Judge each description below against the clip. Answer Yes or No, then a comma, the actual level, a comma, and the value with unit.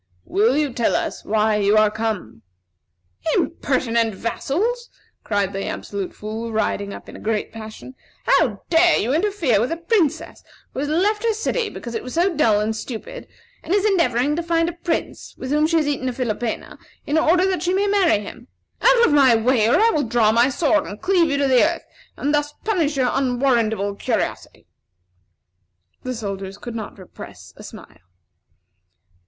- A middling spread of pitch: No, wide, 7.2 semitones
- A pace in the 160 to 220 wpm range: Yes, average, 180 wpm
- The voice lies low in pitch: No, very high, 260 Hz